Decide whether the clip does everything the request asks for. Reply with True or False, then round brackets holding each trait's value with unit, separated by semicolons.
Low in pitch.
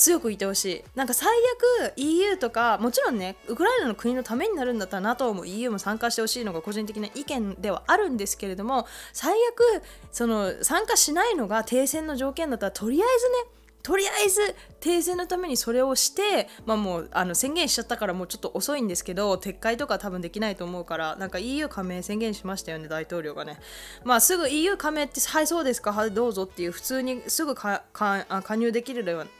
False (235 Hz)